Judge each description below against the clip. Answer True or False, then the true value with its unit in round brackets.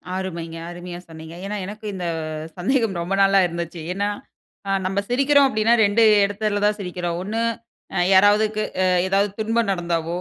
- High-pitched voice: True (195 Hz)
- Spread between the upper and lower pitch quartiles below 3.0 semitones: False (3.5 semitones)